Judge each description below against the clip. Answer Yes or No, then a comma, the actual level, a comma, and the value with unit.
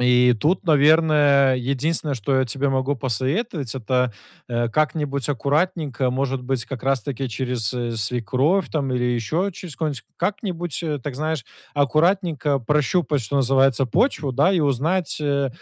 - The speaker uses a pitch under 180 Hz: Yes, medium, 140 Hz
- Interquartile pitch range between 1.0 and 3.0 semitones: No, average, 3.5 semitones